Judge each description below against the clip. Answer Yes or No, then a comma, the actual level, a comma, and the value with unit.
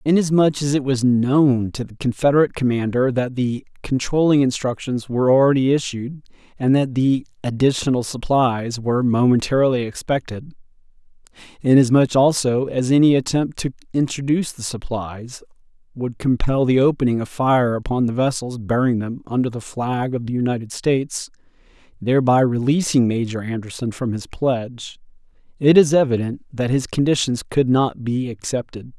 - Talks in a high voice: No, low, 130 Hz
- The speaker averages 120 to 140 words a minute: Yes, slow, 135 wpm